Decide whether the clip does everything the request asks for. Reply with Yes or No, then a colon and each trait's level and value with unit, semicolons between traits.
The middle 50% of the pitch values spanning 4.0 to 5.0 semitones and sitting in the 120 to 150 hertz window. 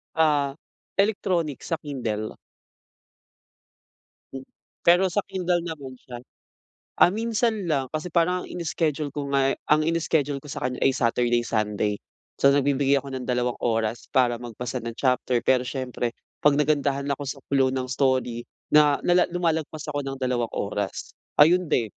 Yes: average, 4.4 semitones; medium, 140 Hz